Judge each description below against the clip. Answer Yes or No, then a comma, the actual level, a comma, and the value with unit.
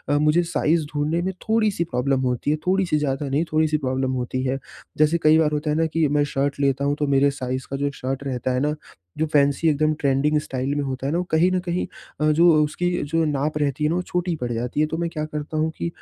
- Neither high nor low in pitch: Yes, medium, 150 Hz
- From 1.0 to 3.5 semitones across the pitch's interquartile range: Yes, average, 2.8 semitones